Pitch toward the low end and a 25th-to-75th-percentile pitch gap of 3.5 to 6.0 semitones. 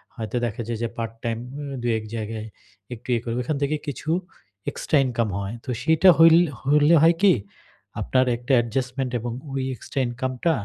Yes: low, 125 Hz; average, 4.0 semitones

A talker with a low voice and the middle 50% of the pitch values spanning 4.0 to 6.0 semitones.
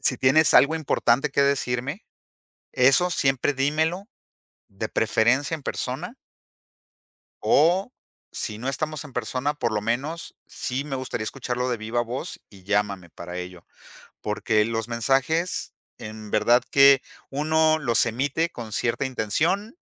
Yes: low, 130 Hz; average, 4.7 semitones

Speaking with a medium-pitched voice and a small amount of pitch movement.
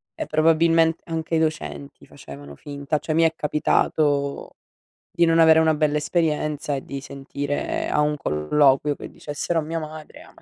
Yes: medium, 150 Hz; narrow, 2.2 semitones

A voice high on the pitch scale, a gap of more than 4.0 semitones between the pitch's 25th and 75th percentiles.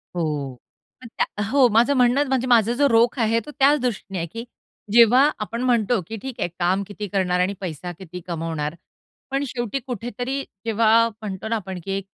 Yes: high, 225 Hz; average, 4.6 semitones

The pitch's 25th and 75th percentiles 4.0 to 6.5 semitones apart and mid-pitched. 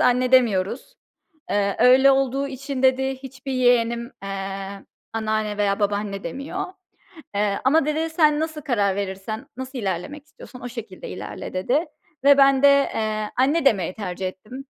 No: average, 5.1 semitones; high, 245 Hz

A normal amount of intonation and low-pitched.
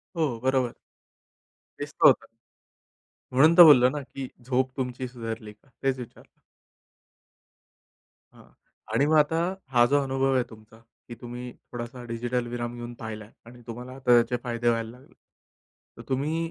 No: narrow, 2.0 semitones; low, 125 Hz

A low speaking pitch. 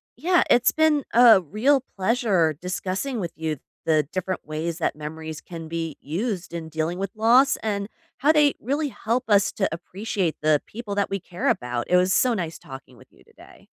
No: high, 190 Hz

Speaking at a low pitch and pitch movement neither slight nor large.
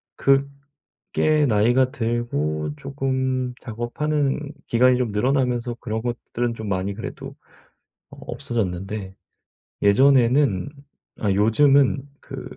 Yes: low, 120 Hz; average, 4.3 semitones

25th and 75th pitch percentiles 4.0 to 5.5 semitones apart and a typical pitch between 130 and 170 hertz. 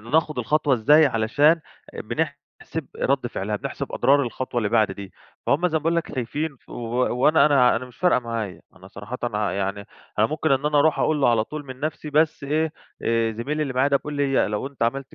Yes: average, 4.6 semitones; low, 135 Hz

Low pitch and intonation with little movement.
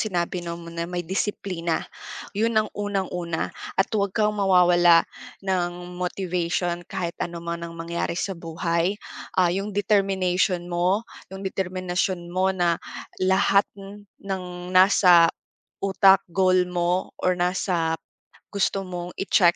No: medium, 180 Hz; narrow, 1.8 semitones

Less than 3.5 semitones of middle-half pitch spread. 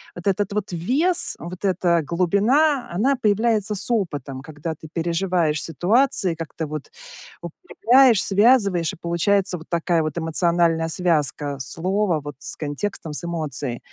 No: average, 4.2 semitones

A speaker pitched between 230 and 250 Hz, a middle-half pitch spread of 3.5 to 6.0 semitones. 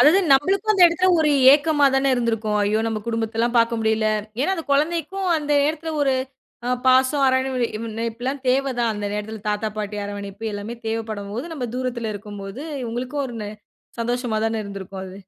Yes: high, 235 Hz; average, 4.5 semitones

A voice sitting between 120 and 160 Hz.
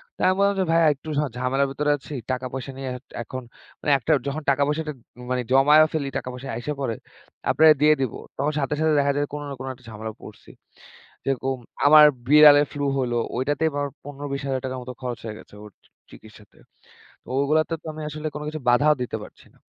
Yes: medium, 140 Hz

